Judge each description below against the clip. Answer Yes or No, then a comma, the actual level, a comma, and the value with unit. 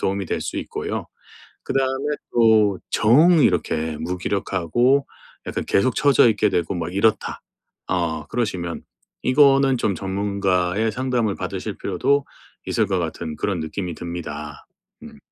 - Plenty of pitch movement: Yes, wide, 6.3 semitones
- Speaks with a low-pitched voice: Yes, low, 100 Hz